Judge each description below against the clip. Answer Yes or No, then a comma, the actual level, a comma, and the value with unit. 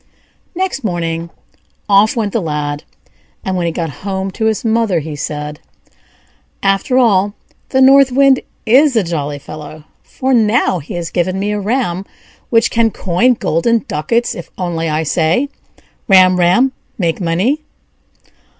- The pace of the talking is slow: No, average, 150 wpm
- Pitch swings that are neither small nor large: No, wide, 5.8 semitones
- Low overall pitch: No, high, 190 Hz